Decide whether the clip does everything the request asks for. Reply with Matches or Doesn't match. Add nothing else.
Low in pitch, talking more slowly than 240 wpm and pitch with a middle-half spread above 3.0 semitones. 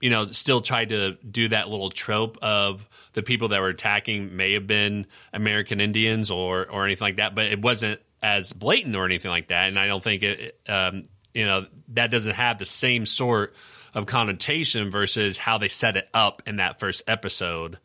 Doesn't match